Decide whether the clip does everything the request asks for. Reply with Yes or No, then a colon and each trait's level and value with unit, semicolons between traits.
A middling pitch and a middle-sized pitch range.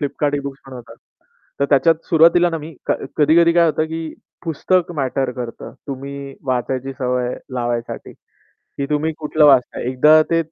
Yes: medium, 145 Hz; average, 3.6 semitones